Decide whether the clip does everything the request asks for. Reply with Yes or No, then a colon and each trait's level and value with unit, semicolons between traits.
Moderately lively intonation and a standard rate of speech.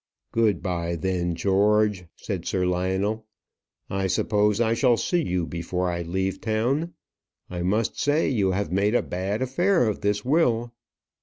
Yes: average, 3.9 semitones; average, 155 wpm